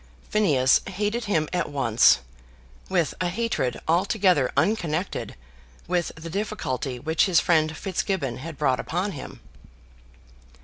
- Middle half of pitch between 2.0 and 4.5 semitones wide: No, average, 5.2 semitones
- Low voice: No, medium, 165 Hz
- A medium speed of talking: No, slow, 120 wpm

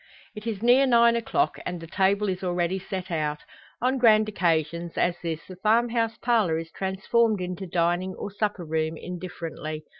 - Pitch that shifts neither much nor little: Yes, average, 4.5 semitones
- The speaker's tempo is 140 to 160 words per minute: No, average, 175 wpm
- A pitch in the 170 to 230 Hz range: Yes, high, 190 Hz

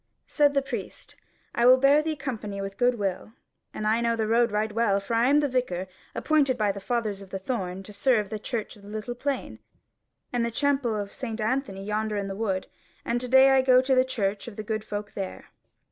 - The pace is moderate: No, fast, 235 wpm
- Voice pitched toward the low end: No, high, 225 Hz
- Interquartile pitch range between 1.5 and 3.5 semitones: No, average, 4.0 semitones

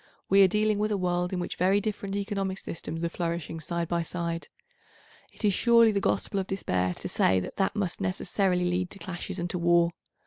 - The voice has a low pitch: No, medium, 180 Hz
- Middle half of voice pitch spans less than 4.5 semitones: Yes, narrow, 2.6 semitones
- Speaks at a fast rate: Yes, fast, 210 wpm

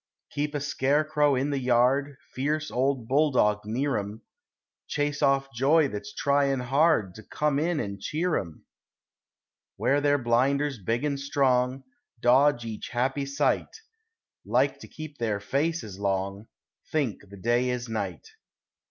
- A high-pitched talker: No, low, 135 Hz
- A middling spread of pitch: Yes, average, 3.9 semitones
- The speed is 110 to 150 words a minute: Yes, average, 140 wpm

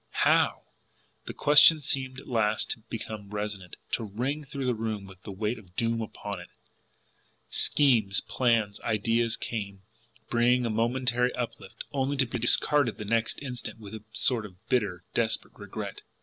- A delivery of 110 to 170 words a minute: Yes, average, 160 wpm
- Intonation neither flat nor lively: Yes, average, 3.2 semitones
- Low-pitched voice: Yes, low, 115 Hz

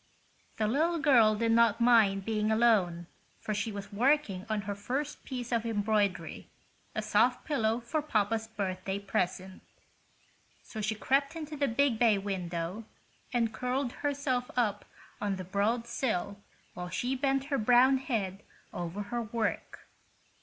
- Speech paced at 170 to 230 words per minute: No, average, 145 wpm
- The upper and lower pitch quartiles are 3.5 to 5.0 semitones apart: Yes, average, 3.8 semitones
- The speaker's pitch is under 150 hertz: No, high, 225 Hz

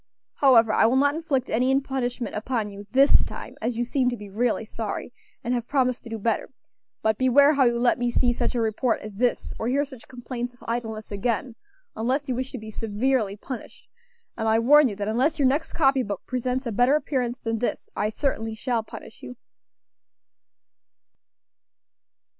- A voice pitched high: Yes, high, 245 Hz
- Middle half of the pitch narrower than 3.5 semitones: Yes, average, 2.8 semitones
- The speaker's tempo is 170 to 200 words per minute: Yes, average, 190 wpm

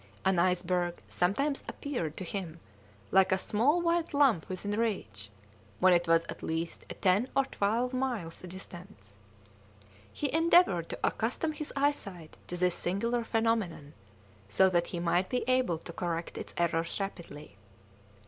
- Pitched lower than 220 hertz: Yes, high, 190 Hz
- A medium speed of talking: Yes, average, 150 wpm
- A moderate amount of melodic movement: No, wide, 6.2 semitones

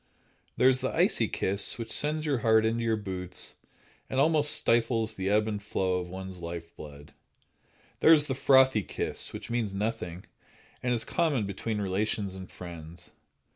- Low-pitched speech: Yes, low, 110 Hz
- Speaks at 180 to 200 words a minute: No, average, 170 wpm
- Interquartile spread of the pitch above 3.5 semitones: Yes, average, 4.8 semitones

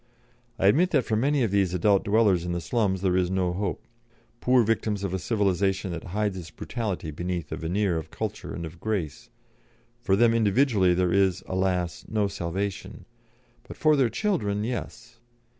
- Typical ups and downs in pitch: Yes, average, 3.7 semitones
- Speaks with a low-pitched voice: Yes, low, 100 Hz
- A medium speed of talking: Yes, average, 175 wpm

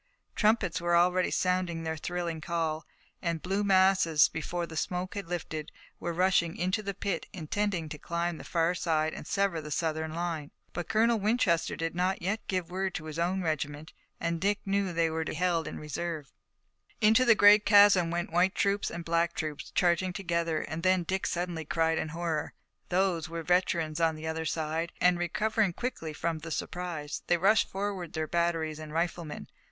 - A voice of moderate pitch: Yes, medium, 170 Hz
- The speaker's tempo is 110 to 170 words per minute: No, average, 190 wpm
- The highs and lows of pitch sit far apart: No, narrow, 2.5 semitones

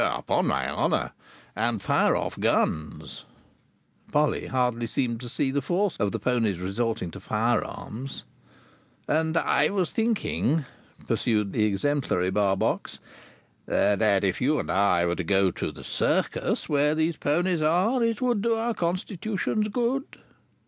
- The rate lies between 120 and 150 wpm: Yes, average, 140 wpm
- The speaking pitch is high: No, low, 135 Hz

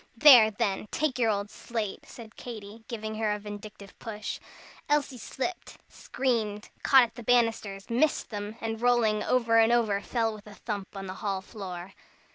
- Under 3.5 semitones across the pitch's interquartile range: Yes, narrow, 2.6 semitones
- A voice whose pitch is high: Yes, high, 220 Hz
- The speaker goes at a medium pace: Yes, average, 170 wpm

